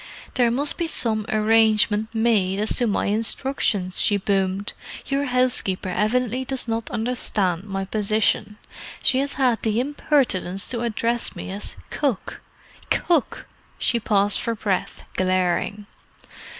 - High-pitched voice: Yes, high, 220 Hz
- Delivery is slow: Yes, slow, 130 wpm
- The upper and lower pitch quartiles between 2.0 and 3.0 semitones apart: No, average, 3.6 semitones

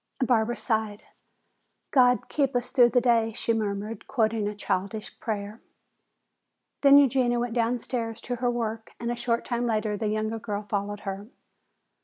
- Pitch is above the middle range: Yes, high, 225 Hz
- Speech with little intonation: Yes, narrow, 2.3 semitones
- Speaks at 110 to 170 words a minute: Yes, average, 155 wpm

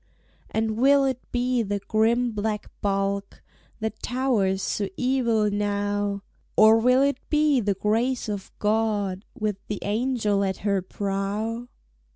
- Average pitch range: Yes, average, 3.3 semitones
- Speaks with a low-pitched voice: No, high, 215 Hz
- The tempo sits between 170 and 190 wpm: No, slow, 135 wpm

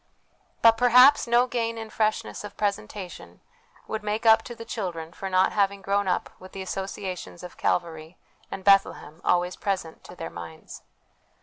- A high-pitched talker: Yes, high, 195 Hz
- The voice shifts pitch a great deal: No, average, 3.7 semitones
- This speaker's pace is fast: No, average, 165 wpm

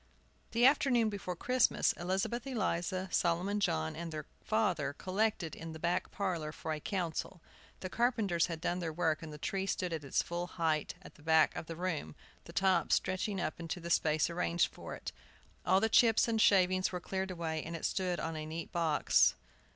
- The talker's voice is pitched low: No, medium, 175 Hz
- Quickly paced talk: No, average, 195 wpm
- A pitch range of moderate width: Yes, average, 3.2 semitones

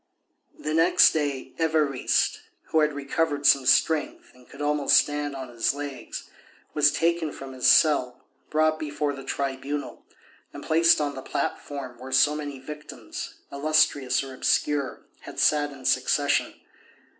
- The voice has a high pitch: No, medium, 145 Hz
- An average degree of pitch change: No, narrow, 2.1 semitones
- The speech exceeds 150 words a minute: No, average, 145 wpm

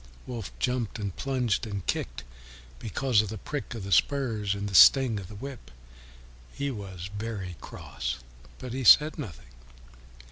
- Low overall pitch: Yes, low, 110 Hz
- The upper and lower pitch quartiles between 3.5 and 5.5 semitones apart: Yes, average, 4.7 semitones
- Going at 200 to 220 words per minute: No, average, 155 wpm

